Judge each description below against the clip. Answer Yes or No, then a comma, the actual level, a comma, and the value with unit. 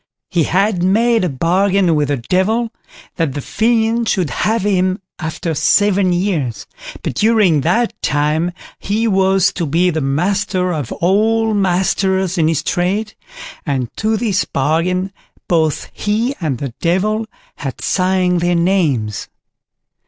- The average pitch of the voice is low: No, medium, 185 Hz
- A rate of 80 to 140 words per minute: Yes, slow, 135 wpm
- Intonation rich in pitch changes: No, average, 4.3 semitones